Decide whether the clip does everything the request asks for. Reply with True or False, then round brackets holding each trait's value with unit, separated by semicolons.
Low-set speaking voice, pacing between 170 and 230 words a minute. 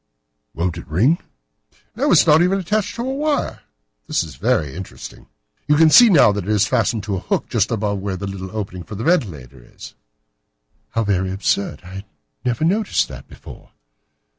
True (105 Hz; 190 wpm)